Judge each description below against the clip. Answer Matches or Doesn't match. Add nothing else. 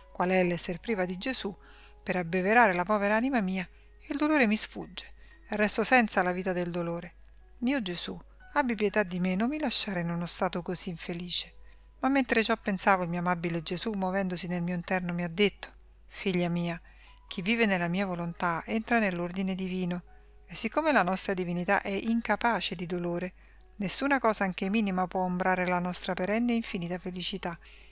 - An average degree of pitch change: Matches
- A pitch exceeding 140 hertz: Matches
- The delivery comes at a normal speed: Doesn't match